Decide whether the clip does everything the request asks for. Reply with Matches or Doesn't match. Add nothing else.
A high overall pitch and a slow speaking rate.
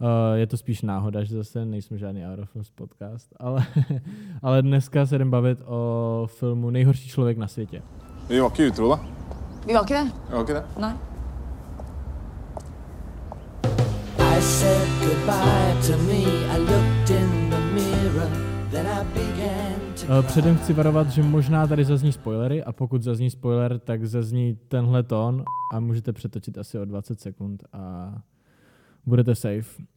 Doesn't match